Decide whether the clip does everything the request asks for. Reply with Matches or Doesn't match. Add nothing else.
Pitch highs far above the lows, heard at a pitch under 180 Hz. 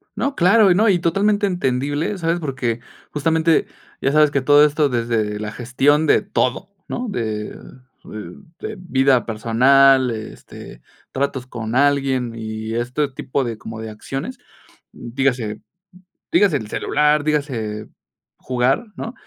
Doesn't match